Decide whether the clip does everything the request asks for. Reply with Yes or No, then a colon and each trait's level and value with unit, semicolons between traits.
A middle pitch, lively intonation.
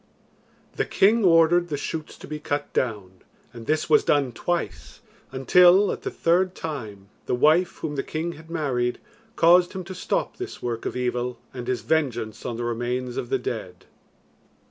Yes: medium, 150 Hz; wide, 6.0 semitones